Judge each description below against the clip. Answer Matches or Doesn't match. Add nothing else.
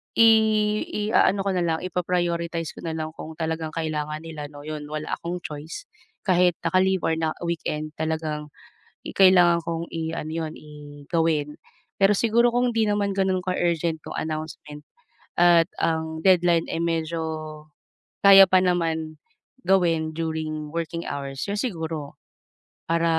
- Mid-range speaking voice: Matches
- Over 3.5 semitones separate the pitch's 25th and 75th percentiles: Doesn't match